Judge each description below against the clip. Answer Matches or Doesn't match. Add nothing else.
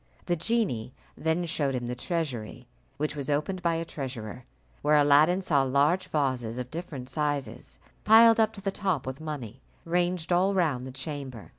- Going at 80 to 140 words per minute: Doesn't match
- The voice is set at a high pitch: Doesn't match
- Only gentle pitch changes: Doesn't match